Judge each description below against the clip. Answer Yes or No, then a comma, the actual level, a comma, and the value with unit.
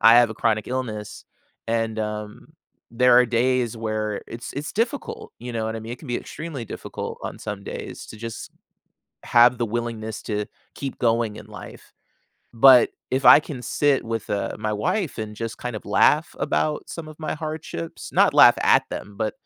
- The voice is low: Yes, low, 115 Hz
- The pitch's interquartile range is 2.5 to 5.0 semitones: Yes, average, 2.8 semitones